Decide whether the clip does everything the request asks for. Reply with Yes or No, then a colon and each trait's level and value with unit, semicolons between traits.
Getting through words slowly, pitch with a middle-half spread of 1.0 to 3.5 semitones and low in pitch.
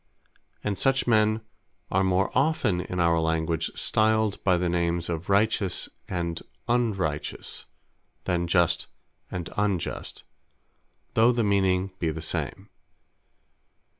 No: slow, 115 wpm; average, 4.1 semitones; very low, 95 Hz